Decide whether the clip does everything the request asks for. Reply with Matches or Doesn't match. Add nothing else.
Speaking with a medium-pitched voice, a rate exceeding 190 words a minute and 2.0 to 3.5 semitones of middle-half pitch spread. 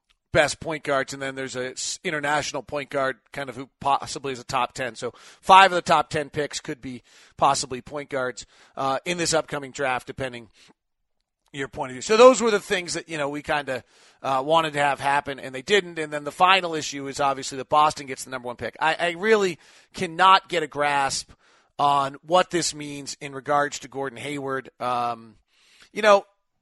Matches